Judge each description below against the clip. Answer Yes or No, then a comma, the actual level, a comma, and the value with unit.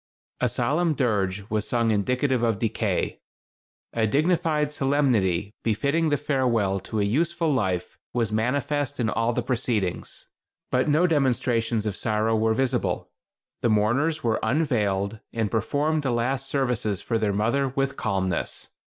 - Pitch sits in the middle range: No, low, 120 Hz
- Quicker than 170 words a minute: No, average, 140 wpm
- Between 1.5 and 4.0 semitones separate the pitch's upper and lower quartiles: No, average, 4.6 semitones